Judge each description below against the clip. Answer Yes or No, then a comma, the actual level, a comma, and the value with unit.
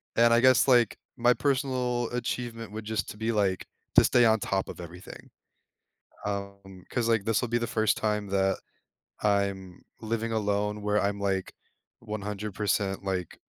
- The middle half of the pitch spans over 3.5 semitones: No, average, 2.8 semitones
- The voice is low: Yes, low, 105 Hz